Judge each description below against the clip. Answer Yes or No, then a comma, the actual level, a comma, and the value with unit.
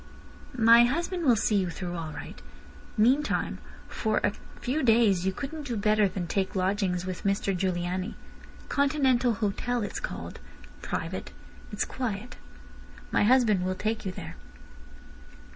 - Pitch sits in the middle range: No, high, 210 Hz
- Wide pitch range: No, average, 4.7 semitones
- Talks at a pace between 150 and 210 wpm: No, average, 140 wpm